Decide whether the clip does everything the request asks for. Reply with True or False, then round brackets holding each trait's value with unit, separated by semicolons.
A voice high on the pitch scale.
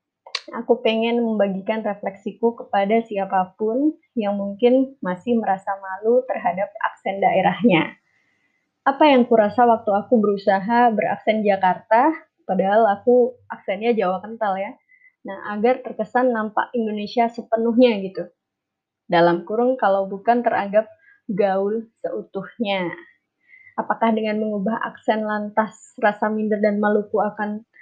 True (220 Hz)